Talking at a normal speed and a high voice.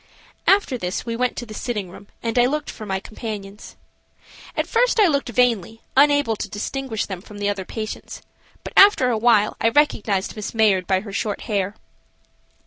Yes: average, 180 wpm; high, 220 Hz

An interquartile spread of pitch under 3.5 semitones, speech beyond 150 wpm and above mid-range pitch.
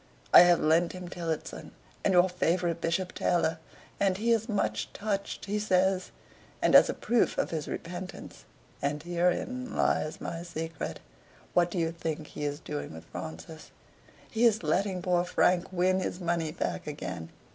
No: average, 2.7 semitones; average, 165 wpm; medium, 175 Hz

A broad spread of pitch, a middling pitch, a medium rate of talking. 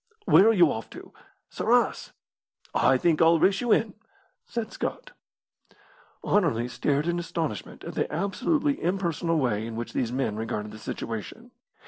Yes: wide, 8.7 semitones; medium, 165 Hz; average, 150 wpm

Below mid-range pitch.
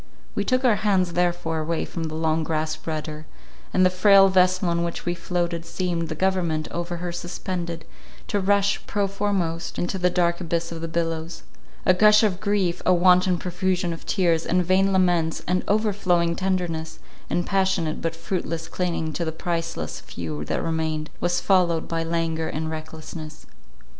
No: medium, 175 Hz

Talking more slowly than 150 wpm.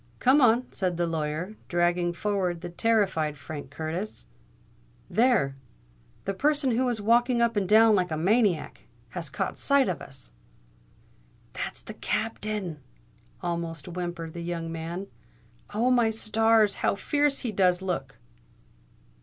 Yes: slow, 135 wpm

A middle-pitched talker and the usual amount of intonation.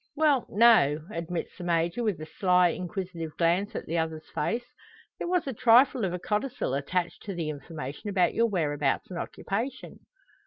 No: medium, 180 Hz; wide, 5.7 semitones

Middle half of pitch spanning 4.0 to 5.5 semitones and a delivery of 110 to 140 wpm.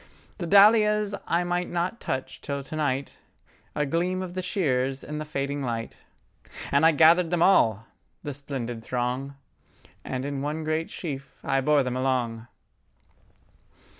Yes: average, 4.6 semitones; slow, 135 wpm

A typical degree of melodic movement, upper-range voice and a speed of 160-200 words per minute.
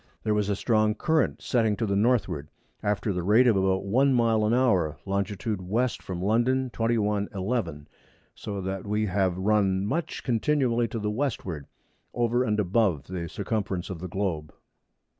No: average, 3.6 semitones; low, 105 Hz; average, 165 wpm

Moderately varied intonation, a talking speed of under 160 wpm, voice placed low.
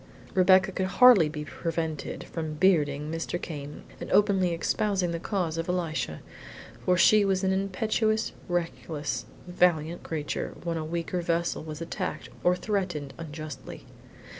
No: average, 3.2 semitones; average, 140 wpm; medium, 170 Hz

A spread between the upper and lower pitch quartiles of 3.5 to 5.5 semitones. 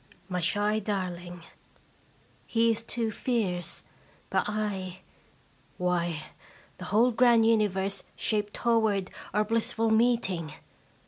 Yes: average, 3.9 semitones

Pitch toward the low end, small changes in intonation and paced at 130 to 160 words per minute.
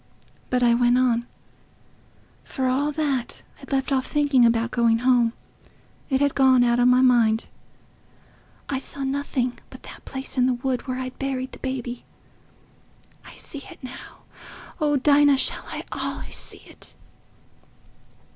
No: very high, 255 Hz; narrow, 1.9 semitones; average, 145 wpm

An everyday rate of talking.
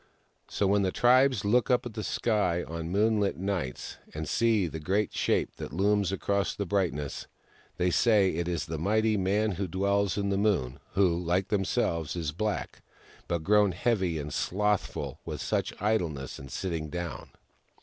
Yes: average, 170 wpm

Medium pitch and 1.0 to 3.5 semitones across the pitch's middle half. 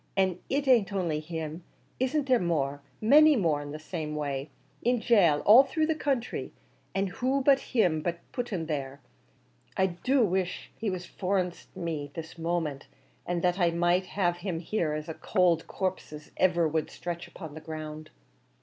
No: medium, 175 Hz; wide, 5.4 semitones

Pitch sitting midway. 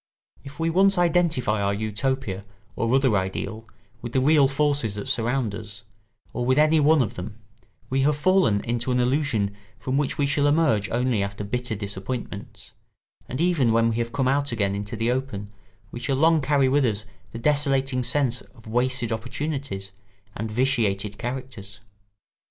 No: low, 125 Hz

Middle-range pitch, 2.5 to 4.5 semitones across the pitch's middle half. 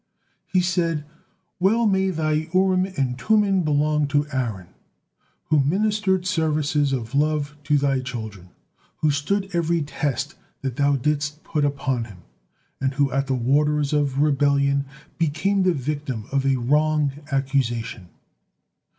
Yes: medium, 145 Hz; average, 3.0 semitones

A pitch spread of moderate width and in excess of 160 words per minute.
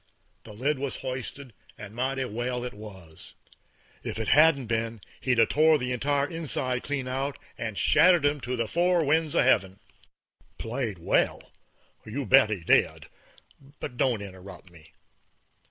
No: average, 4.6 semitones; average, 155 wpm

